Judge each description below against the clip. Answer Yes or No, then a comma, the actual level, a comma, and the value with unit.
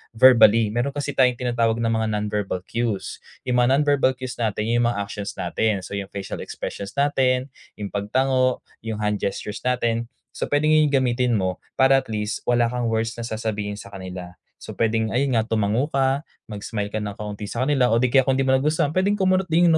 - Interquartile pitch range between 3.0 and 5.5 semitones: Yes, average, 4.0 semitones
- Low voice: Yes, low, 115 Hz